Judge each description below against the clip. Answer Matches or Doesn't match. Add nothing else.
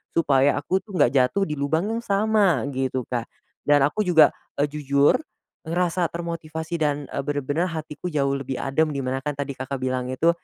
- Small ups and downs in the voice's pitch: Doesn't match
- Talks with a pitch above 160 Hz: Doesn't match